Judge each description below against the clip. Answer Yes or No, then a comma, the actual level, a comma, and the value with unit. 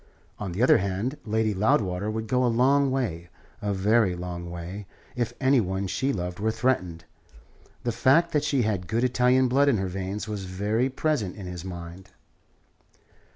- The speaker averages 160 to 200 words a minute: Yes, average, 175 wpm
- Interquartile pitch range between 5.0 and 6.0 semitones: Yes, average, 5.3 semitones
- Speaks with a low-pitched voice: Yes, low, 105 Hz